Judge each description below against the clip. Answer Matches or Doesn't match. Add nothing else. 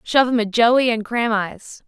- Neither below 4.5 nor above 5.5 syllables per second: Doesn't match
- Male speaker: Doesn't match